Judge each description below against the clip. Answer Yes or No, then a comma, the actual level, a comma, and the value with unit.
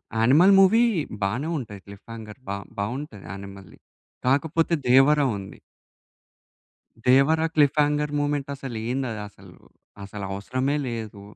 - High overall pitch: No, low, 130 Hz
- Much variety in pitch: Yes, wide, 6.1 semitones